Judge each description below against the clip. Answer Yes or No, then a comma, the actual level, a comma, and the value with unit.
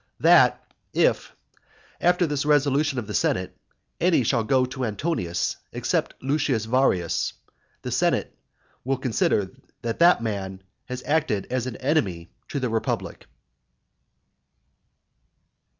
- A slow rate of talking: Yes, slow, 120 wpm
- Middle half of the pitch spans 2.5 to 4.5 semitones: No, average, 5.1 semitones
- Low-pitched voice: Yes, low, 130 Hz